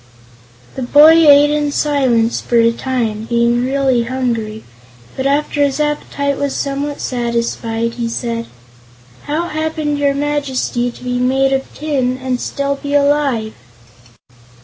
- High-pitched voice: Yes, very high, 270 Hz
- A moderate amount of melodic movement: Yes, average, 3.3 semitones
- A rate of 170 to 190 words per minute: No, slow, 135 wpm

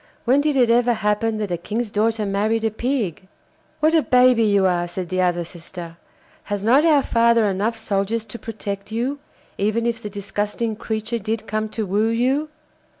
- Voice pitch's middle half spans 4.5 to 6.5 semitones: No, average, 2.7 semitones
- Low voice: No, high, 220 Hz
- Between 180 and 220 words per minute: Yes, average, 185 wpm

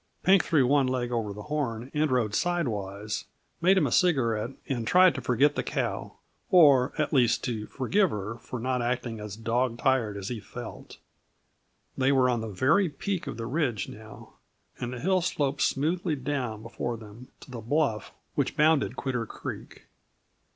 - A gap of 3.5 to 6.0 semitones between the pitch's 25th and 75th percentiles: Yes, average, 4.5 semitones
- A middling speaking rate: Yes, average, 175 wpm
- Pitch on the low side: Yes, low, 125 Hz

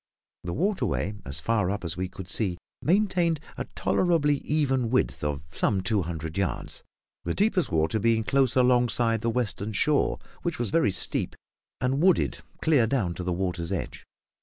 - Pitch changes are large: Yes, wide, 7.8 semitones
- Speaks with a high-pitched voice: No, low, 115 Hz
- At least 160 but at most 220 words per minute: Yes, average, 165 wpm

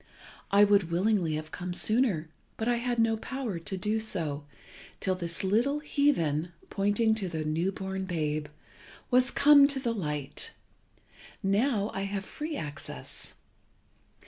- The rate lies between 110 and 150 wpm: Yes, average, 145 wpm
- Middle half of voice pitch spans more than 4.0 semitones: Yes, wide, 5.5 semitones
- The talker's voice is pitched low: No, high, 195 Hz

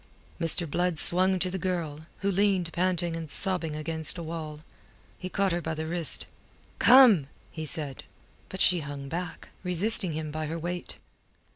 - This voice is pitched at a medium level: Yes, medium, 170 Hz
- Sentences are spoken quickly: No, average, 165 wpm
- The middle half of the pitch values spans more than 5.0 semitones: No, narrow, 2.6 semitones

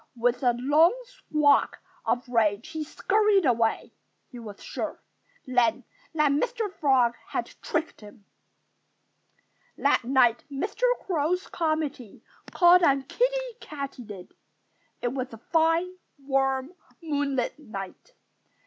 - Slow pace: Yes, slow, 110 wpm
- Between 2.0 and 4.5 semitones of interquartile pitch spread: No, average, 5.3 semitones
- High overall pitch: Yes, very high, 280 Hz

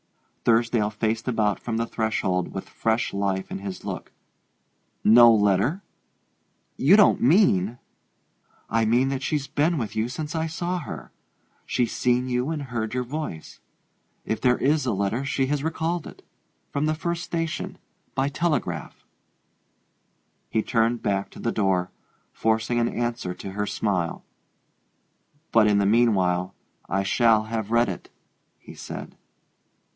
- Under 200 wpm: Yes, average, 150 wpm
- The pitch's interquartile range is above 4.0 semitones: Yes, average, 4.9 semitones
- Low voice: Yes, low, 115 Hz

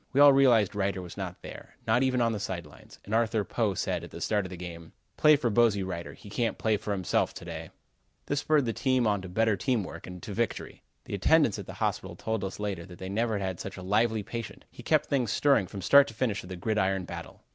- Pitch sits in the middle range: No, low, 105 Hz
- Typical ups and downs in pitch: Yes, average, 3.8 semitones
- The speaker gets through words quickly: Yes, fast, 255 wpm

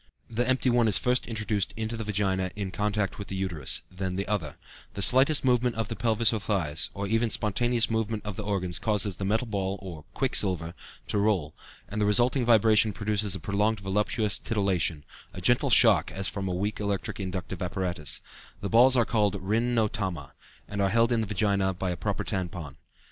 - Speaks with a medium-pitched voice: No, low, 105 Hz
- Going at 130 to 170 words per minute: No, average, 200 wpm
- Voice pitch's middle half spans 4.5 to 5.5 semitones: No, average, 2.9 semitones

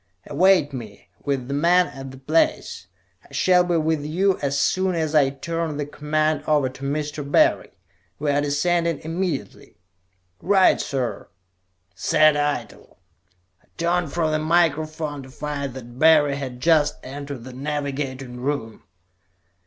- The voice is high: No, medium, 145 Hz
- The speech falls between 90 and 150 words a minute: Yes, average, 145 wpm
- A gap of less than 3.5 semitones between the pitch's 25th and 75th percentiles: Yes, average, 2.9 semitones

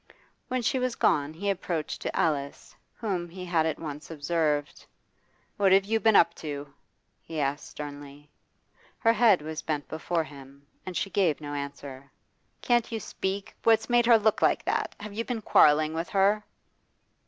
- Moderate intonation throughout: No, wide, 6.1 semitones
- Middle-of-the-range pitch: Yes, medium, 165 Hz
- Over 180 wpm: No, average, 170 wpm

